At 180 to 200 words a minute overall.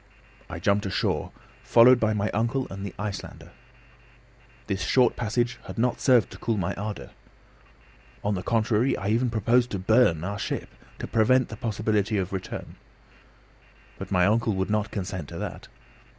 No: average, 165 wpm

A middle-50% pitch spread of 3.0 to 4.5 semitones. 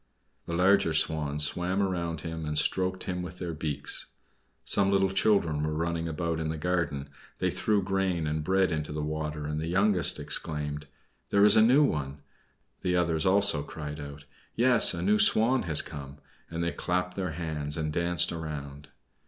Yes: average, 3.5 semitones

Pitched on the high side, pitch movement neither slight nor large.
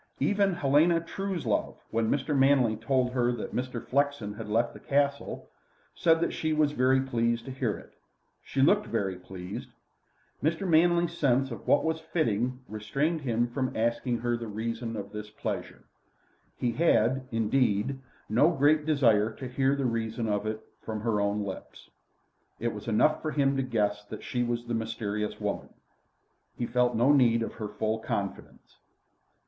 No: low, 120 Hz; average, 4.2 semitones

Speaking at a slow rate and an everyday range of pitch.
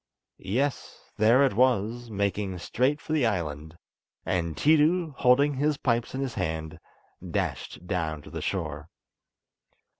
No: slow, 130 wpm; wide, 8.2 semitones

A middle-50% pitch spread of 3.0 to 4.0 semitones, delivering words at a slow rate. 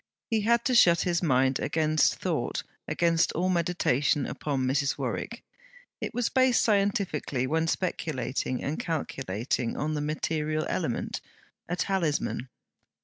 No: average, 4.5 semitones; slow, 130 wpm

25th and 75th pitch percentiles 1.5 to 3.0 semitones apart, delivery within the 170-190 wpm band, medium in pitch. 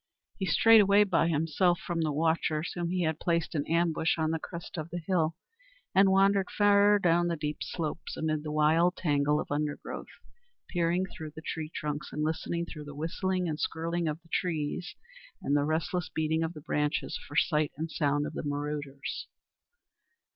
Yes: narrow, 2.5 semitones; average, 185 wpm; medium, 160 Hz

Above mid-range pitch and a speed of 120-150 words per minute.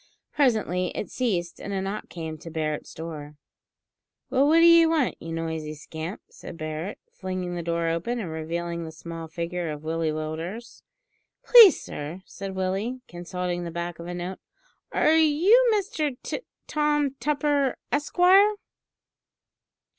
No: medium, 180 Hz; average, 145 wpm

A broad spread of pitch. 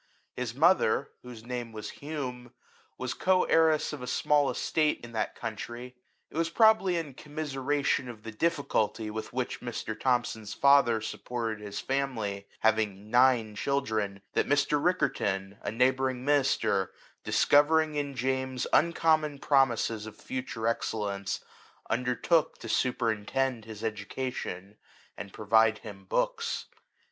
No: average, 4.5 semitones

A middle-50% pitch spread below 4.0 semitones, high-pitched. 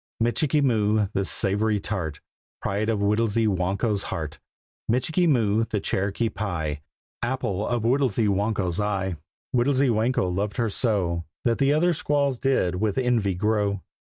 No: average, 3.6 semitones; low, 105 Hz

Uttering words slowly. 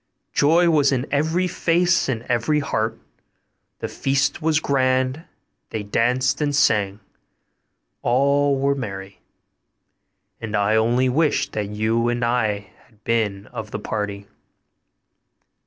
Yes: slow, 125 wpm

